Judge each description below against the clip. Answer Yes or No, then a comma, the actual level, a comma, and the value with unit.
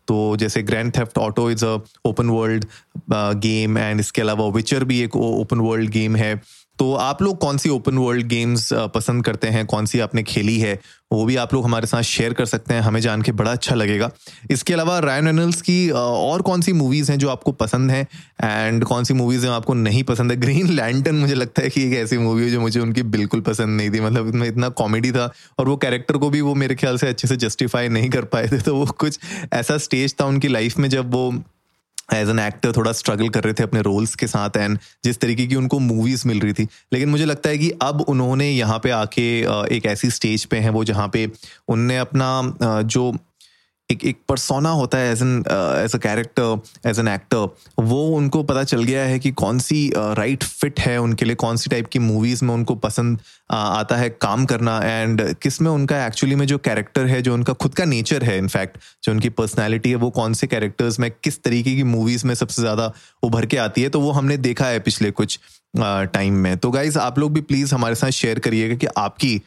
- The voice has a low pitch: Yes, low, 120 Hz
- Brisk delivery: Yes, fast, 230 wpm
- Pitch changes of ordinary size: Yes, average, 3.5 semitones